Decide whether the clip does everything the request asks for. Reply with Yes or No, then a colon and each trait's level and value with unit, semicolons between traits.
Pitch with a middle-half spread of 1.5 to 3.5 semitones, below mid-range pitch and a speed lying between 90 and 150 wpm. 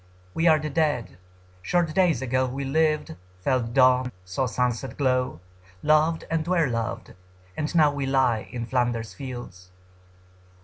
No: average, 4.0 semitones; low, 130 Hz; average, 140 wpm